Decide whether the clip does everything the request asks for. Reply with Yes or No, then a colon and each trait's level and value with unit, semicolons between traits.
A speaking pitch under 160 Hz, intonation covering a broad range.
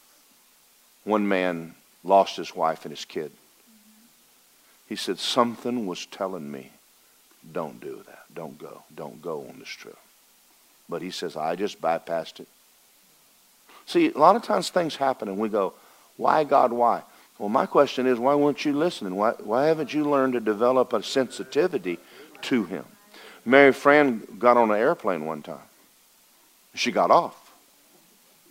Yes: low, 135 Hz; wide, 5.9 semitones